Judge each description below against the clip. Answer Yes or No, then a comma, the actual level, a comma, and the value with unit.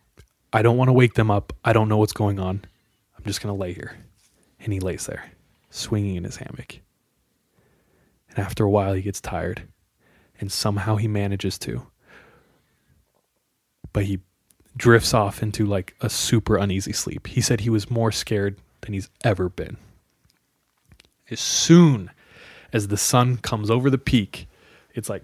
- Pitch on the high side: No, low, 105 Hz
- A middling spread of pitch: Yes, average, 3.0 semitones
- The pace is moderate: Yes, average, 165 wpm